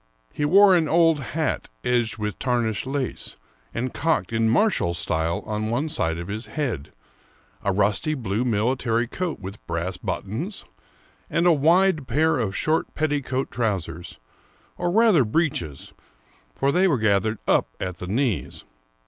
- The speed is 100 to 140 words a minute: No, average, 155 wpm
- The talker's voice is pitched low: Yes, low, 120 Hz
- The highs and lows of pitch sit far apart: Yes, wide, 7.2 semitones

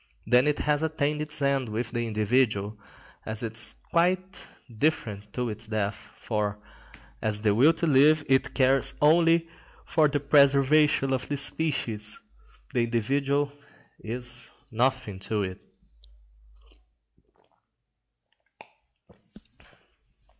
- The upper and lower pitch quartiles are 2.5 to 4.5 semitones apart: No, average, 5.0 semitones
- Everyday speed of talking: No, slow, 110 wpm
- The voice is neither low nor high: No, low, 130 Hz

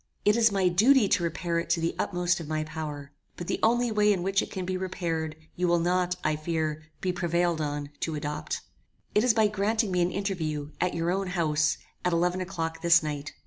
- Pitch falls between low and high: Yes, medium, 175 Hz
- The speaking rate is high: Yes, fast, 220 wpm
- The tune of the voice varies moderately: Yes, average, 3.0 semitones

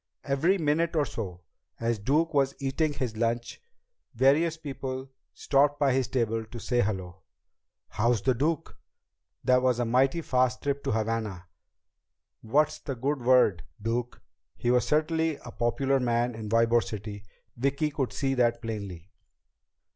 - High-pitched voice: No, low, 125 Hz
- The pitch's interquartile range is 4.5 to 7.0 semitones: No, average, 3.7 semitones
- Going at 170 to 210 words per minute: No, average, 145 wpm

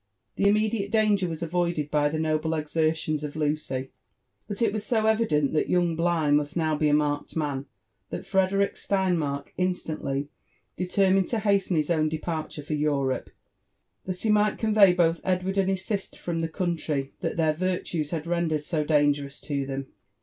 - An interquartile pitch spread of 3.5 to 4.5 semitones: Yes, average, 4.1 semitones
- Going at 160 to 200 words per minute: Yes, average, 170 wpm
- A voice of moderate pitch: Yes, medium, 165 Hz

